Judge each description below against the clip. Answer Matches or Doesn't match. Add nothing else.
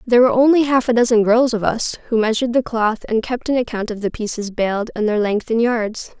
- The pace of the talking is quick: Matches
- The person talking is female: Matches